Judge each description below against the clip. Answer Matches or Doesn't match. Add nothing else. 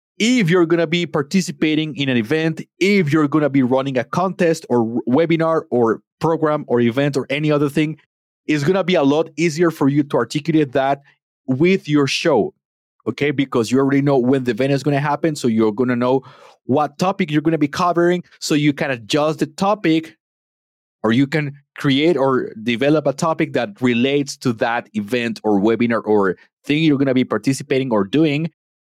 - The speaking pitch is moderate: Matches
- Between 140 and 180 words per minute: Doesn't match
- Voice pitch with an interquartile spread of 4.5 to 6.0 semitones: Doesn't match